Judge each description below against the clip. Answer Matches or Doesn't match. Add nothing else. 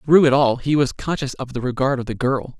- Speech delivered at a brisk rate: Matches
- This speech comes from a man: Matches